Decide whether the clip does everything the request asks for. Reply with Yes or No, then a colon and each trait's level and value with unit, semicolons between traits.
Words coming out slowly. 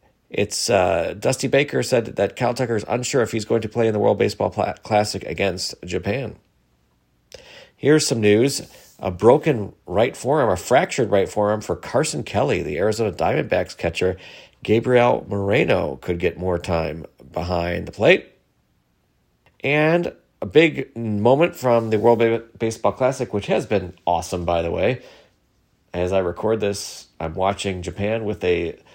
No: average, 160 wpm